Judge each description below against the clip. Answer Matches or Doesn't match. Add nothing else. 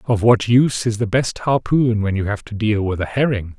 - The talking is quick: Matches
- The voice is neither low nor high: Doesn't match